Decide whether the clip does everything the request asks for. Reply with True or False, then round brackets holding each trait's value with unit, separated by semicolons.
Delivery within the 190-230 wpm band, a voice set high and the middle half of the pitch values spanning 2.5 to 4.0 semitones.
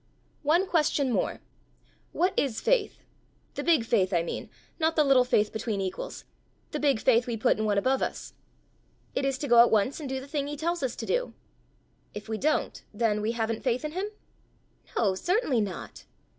False (195 wpm; 260 Hz; 5.6 semitones)